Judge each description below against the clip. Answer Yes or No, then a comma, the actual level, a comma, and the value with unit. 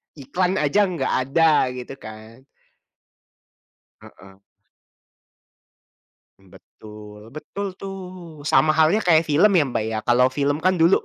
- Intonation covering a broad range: Yes, wide, 6.7 semitones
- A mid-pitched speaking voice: Yes, medium, 150 Hz